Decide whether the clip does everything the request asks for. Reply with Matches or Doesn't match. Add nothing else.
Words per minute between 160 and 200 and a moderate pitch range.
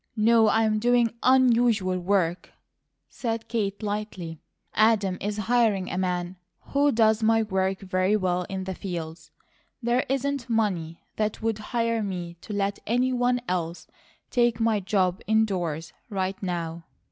Doesn't match